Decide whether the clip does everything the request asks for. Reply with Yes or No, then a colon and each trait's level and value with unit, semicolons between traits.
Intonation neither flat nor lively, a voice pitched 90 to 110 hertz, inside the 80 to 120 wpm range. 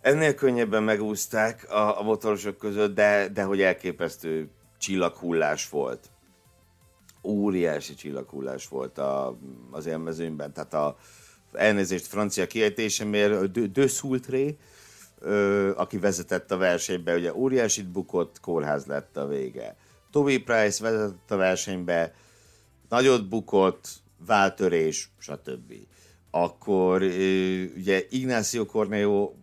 Yes: average, 3.8 semitones; low, 100 Hz; average, 110 wpm